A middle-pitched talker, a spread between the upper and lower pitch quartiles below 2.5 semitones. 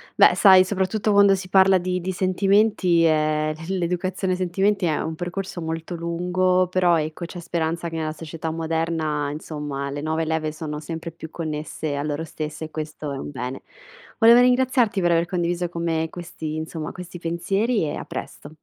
No: medium, 170 Hz; average, 2.9 semitones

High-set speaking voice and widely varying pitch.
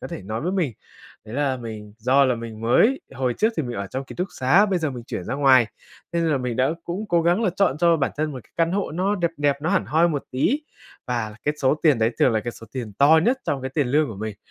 No: medium, 140 Hz; wide, 5.8 semitones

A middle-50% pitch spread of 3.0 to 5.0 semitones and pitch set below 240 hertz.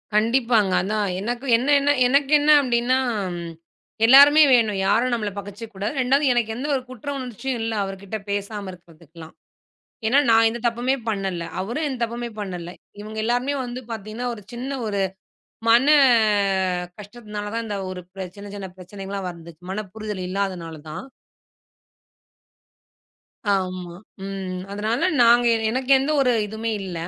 Yes: average, 3.9 semitones; high, 220 Hz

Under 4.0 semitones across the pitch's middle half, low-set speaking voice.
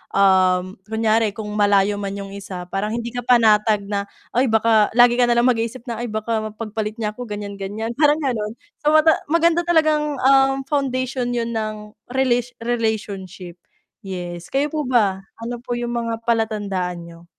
No: average, 3.3 semitones; high, 225 Hz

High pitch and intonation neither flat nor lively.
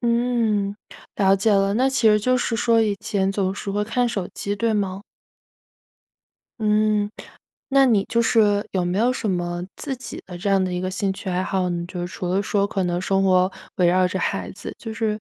Yes: high, 200 Hz; average, 3.1 semitones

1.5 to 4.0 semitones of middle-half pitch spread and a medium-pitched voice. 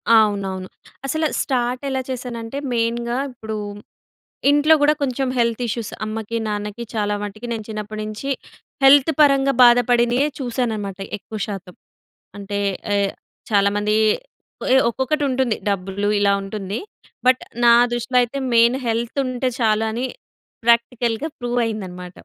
No: average, 3.2 semitones; high, 230 Hz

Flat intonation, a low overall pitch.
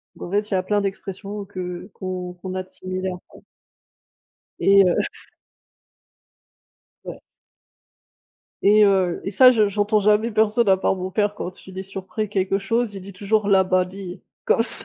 No: narrow, 1.9 semitones; high, 195 Hz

